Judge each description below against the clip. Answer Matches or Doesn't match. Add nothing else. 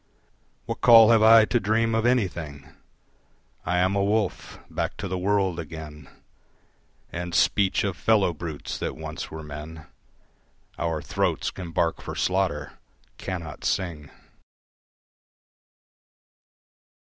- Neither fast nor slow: Doesn't match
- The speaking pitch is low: Matches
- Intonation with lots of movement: Doesn't match